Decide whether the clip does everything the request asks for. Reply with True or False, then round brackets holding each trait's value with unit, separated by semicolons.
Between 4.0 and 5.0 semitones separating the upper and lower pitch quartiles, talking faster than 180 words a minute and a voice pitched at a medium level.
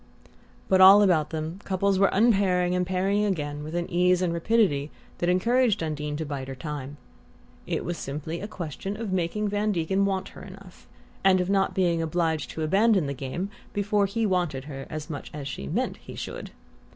True (4.3 semitones; 190 wpm; 180 Hz)